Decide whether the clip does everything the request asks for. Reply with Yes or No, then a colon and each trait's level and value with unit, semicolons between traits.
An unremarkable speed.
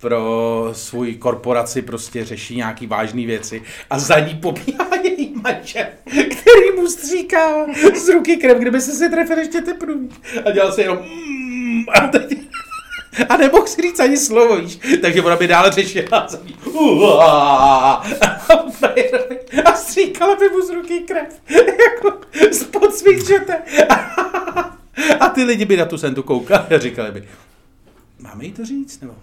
Yes: average, 155 wpm